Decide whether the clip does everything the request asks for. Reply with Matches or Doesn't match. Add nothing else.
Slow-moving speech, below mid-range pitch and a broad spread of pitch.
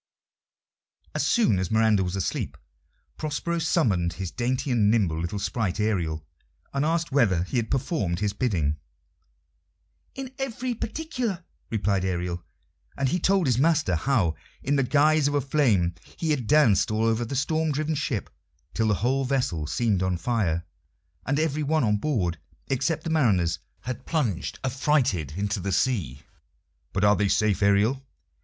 Doesn't match